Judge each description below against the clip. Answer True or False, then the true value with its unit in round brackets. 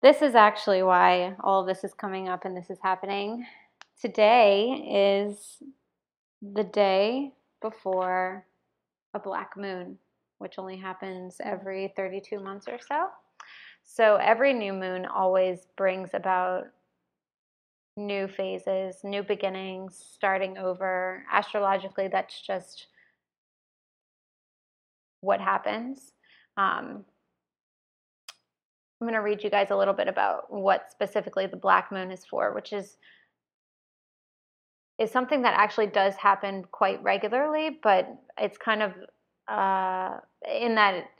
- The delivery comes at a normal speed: False (120 wpm)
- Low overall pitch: False (195 Hz)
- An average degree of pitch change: False (2.1 semitones)